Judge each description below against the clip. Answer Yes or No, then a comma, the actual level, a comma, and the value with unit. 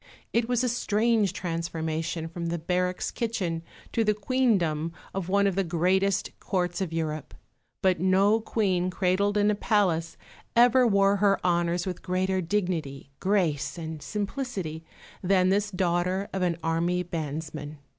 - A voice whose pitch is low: No, medium, 185 Hz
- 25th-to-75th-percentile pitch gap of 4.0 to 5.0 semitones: No, average, 3.4 semitones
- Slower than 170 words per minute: Yes, average, 145 wpm